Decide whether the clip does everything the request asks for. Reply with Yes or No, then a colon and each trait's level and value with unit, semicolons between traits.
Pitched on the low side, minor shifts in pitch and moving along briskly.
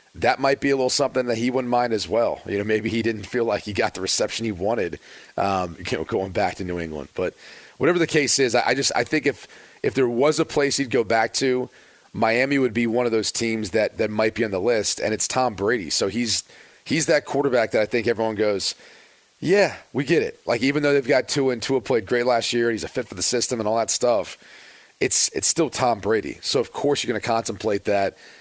No: low, 115 Hz; average, 3.3 semitones; fast, 255 wpm